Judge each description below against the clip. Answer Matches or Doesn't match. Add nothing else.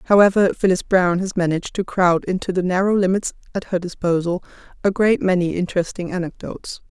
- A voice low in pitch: Doesn't match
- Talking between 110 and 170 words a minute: Matches